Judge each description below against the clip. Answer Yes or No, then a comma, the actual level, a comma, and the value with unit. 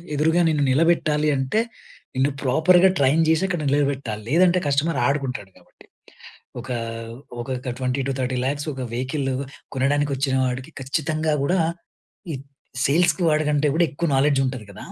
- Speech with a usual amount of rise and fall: Yes, average, 3.2 semitones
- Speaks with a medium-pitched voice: Yes, medium, 145 Hz